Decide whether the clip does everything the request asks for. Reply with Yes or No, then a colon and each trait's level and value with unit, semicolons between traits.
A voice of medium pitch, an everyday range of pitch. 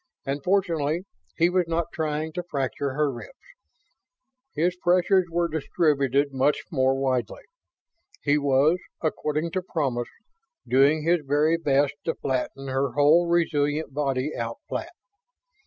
Yes: medium, 150 Hz; average, 3.6 semitones